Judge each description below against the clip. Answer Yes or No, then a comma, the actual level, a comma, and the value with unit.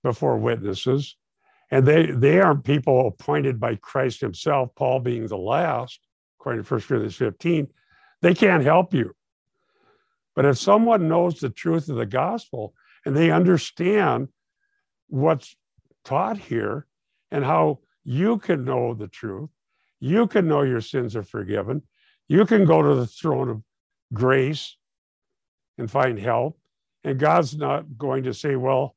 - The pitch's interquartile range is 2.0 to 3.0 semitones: No, average, 5.0 semitones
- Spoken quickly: No, average, 145 wpm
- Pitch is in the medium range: Yes, medium, 145 Hz